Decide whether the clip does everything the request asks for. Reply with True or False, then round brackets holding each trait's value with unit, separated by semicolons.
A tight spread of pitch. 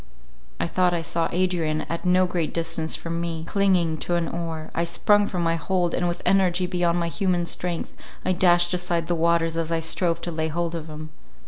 True (1.4 semitones)